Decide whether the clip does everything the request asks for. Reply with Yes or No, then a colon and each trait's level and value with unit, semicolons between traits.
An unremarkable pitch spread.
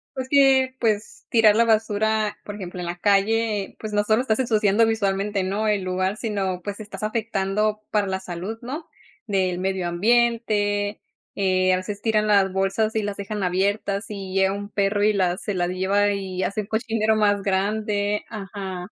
No: narrow, 2.1 semitones